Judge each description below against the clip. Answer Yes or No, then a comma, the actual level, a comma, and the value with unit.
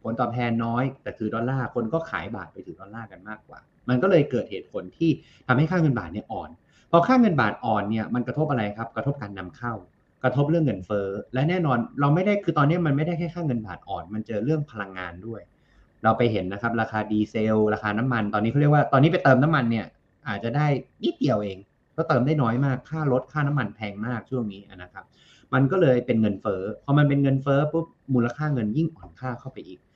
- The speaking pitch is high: No, low, 125 Hz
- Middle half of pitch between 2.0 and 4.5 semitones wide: No, average, 5.0 semitones